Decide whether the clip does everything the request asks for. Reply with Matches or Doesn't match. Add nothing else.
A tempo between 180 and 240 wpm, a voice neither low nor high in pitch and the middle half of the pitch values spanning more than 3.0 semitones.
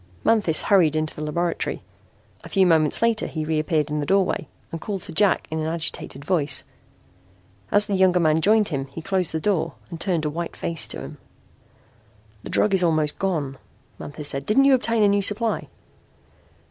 Matches